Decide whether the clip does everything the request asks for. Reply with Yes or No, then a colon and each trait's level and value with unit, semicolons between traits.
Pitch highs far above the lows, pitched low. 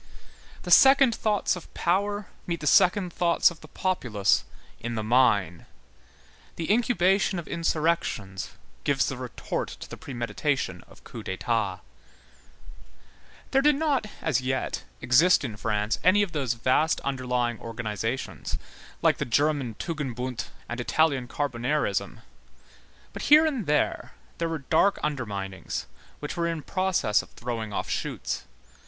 No: wide, 7.0 semitones; medium, 145 Hz